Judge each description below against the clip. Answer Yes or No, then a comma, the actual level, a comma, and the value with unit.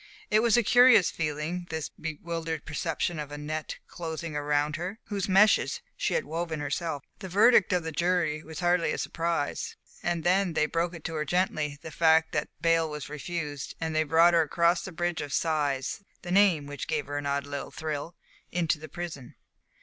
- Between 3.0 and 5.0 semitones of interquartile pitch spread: No, narrow, 2.6 semitones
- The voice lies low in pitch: No, medium, 165 Hz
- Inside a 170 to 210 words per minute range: Yes, average, 195 wpm